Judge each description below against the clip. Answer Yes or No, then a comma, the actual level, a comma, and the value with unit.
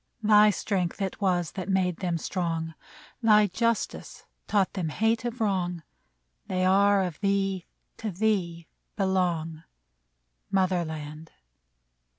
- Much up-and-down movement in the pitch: No, average, 3.0 semitones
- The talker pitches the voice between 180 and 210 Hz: Yes, medium, 185 Hz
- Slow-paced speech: Yes, slow, 120 wpm